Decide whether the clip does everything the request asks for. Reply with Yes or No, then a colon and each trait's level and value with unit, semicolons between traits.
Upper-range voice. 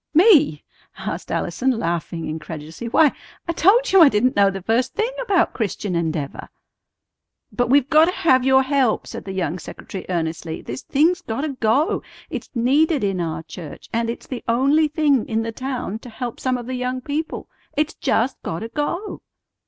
Yes: very high, 250 Hz